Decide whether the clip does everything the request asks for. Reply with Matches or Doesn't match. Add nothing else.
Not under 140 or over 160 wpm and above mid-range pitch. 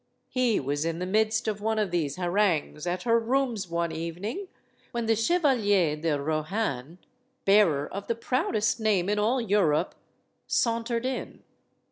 Matches